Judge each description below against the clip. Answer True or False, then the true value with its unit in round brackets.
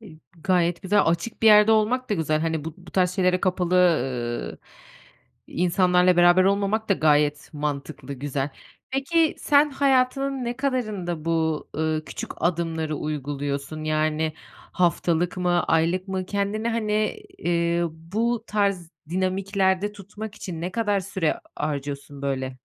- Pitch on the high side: False (180 Hz)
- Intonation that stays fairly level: False (4.9 semitones)